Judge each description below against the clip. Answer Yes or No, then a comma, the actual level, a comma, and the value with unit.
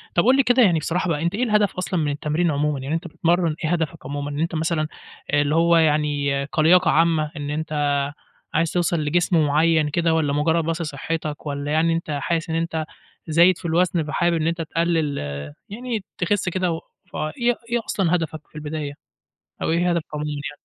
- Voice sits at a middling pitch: Yes, medium, 160 Hz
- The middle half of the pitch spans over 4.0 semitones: No, narrow, 2.4 semitones